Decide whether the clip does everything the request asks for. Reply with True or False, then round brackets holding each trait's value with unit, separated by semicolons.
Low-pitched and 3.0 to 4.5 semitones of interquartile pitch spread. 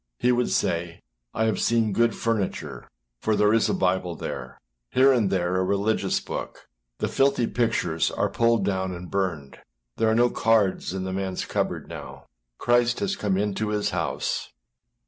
True (105 Hz; 3.7 semitones)